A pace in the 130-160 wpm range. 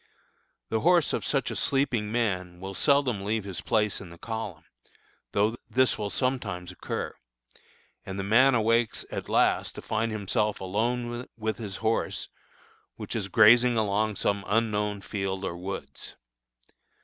Yes: average, 150 wpm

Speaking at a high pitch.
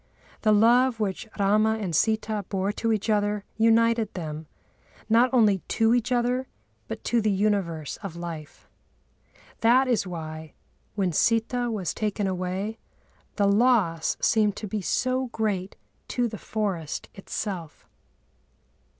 Yes: high, 210 Hz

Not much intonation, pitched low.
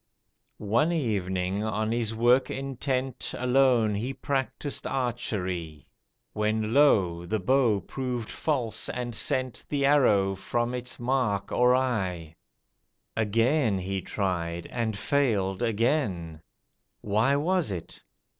No: average, 5.0 semitones; low, 115 Hz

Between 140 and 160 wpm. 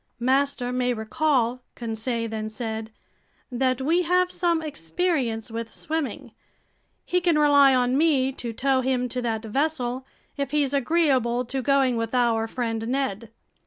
Yes: average, 145 wpm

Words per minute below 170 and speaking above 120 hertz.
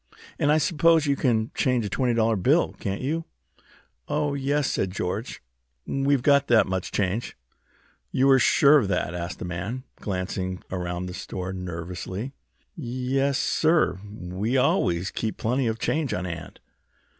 No: average, 155 wpm; low, 115 Hz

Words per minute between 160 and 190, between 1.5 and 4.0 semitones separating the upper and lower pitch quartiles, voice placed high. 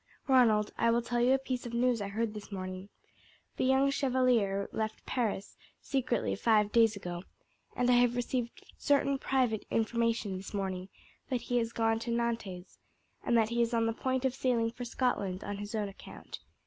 Yes: average, 185 wpm; average, 2.9 semitones; high, 230 Hz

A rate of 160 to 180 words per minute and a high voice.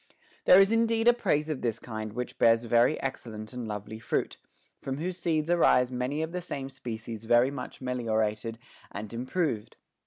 No: average, 175 wpm; low, 125 Hz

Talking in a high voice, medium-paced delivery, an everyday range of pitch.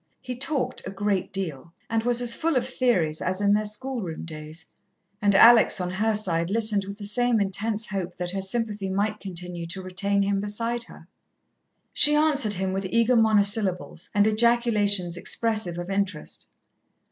Yes: high, 205 Hz; average, 170 wpm; average, 3.5 semitones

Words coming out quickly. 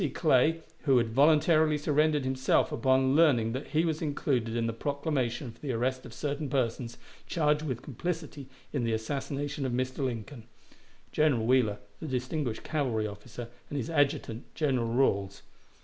No: average, 155 wpm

